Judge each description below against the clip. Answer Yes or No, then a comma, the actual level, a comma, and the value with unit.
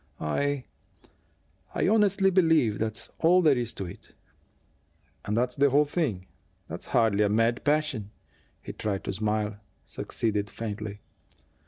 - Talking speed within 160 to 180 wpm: No, slow, 135 wpm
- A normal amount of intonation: No, wide, 6.3 semitones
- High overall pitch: No, low, 115 Hz